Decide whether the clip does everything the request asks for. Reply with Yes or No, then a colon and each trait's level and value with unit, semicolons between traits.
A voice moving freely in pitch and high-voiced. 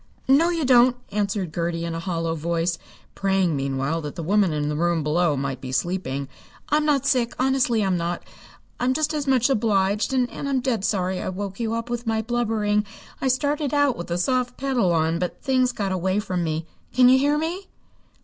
Yes: wide, 7.1 semitones; high, 205 Hz